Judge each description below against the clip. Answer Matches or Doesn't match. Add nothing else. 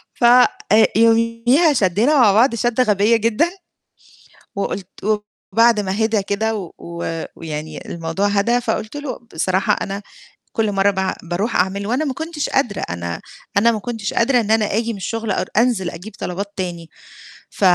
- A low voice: Doesn't match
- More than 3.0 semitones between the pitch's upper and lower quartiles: Matches